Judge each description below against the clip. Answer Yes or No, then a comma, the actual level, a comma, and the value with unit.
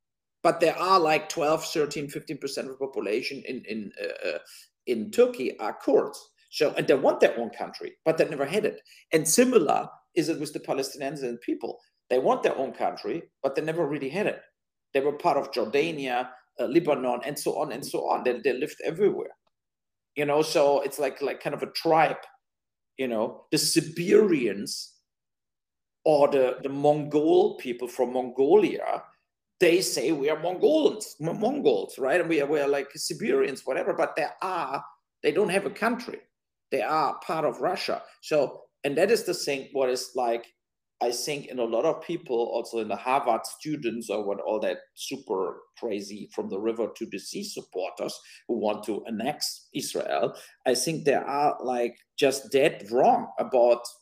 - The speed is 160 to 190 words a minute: Yes, average, 180 wpm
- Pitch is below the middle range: No, medium, 155 Hz